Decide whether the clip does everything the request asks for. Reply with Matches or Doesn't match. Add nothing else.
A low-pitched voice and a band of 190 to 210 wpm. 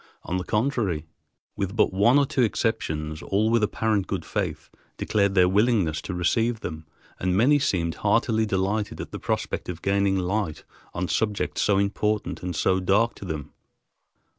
Doesn't match